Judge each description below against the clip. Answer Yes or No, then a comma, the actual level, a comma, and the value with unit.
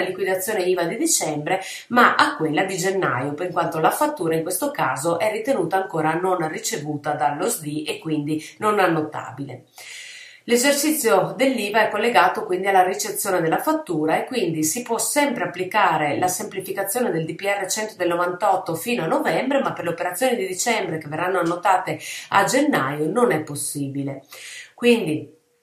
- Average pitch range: No, wide, 6.2 semitones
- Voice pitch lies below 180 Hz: No, medium, 185 Hz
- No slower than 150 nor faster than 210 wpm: Yes, average, 155 wpm